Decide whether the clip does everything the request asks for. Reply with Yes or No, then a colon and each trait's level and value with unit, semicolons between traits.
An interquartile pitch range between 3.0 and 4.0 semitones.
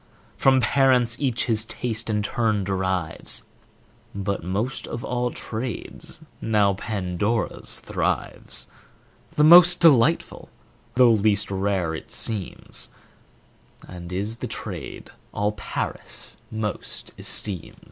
Yes: average, 3.7 semitones